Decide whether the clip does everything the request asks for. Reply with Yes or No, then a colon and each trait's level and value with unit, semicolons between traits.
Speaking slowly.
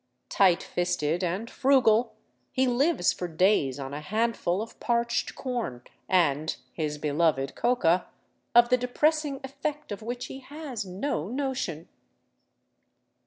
Yes: slow, 125 wpm